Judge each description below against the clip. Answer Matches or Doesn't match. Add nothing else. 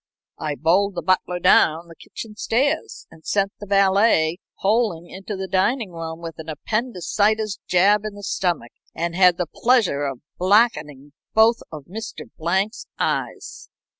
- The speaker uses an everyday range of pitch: Matches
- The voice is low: Doesn't match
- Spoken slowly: Doesn't match